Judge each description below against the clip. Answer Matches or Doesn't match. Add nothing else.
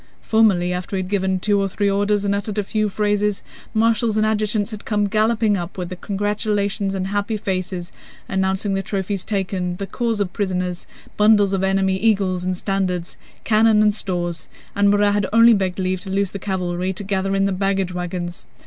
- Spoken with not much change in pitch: Matches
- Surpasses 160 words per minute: Matches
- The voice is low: Doesn't match